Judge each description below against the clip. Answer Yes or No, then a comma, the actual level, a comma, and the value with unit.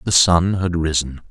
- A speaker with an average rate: Yes, average, 185 wpm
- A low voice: Yes, very low, 85 Hz